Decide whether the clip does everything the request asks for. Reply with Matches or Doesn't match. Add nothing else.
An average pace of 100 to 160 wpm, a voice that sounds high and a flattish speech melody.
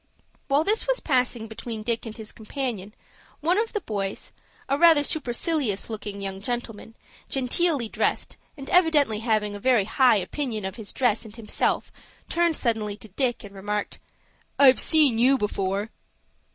Doesn't match